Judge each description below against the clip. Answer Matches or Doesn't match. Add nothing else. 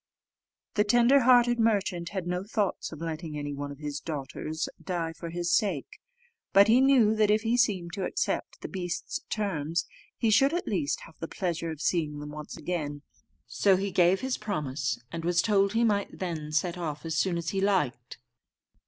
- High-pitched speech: Doesn't match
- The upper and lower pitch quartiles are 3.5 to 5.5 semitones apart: Matches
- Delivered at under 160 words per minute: Doesn't match